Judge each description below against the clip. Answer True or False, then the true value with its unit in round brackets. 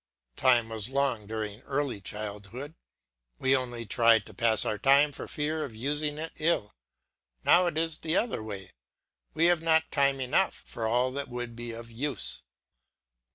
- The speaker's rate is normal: True (165 wpm)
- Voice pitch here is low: True (130 Hz)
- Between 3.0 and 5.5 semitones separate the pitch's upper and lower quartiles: True (4.7 semitones)